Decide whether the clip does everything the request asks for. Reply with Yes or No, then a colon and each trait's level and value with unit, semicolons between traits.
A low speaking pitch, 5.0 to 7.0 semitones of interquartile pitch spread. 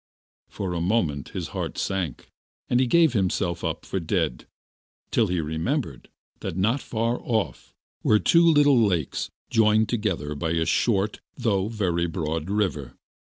Yes: very low, 95 Hz; wide, 5.6 semitones